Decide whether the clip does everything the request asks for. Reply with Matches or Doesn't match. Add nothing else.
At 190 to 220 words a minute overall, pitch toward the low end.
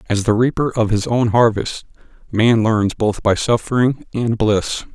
Doesn't match